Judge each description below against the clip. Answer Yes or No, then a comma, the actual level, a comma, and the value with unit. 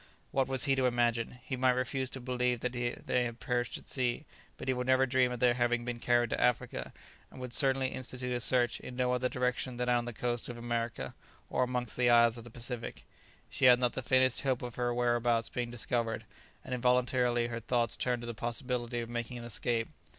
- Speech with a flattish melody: Yes, narrow, 1.0 semitones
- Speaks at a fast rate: Yes, fast, 220 wpm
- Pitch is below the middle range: Yes, low, 125 Hz